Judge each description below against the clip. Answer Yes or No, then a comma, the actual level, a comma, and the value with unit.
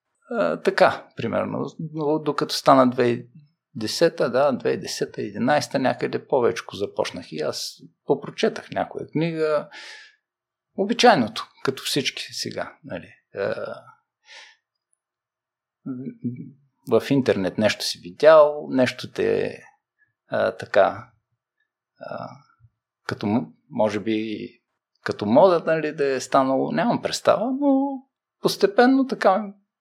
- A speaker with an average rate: No, slow, 95 wpm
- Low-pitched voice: No, medium, 165 Hz